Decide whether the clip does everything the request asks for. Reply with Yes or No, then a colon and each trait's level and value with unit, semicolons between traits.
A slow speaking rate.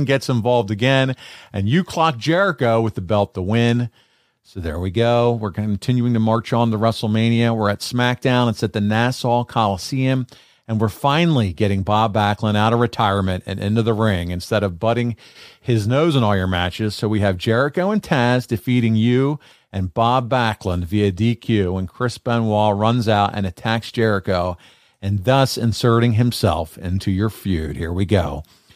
No: average, 175 wpm